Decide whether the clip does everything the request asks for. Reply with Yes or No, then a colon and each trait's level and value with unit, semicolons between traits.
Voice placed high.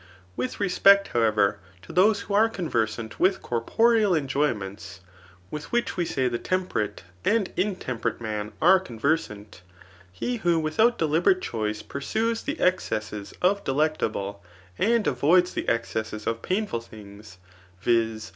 No: medium, 140 Hz